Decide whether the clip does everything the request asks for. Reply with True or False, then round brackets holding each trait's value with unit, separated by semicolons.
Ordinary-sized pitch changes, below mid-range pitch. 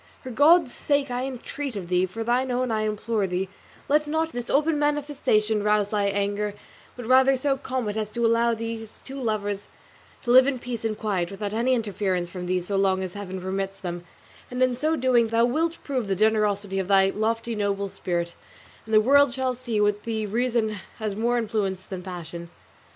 False (4.2 semitones; 220 Hz)